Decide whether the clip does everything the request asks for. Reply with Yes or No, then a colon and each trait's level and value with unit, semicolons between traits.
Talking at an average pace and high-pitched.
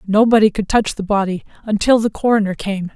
Yes: average, 185 wpm; high, 210 Hz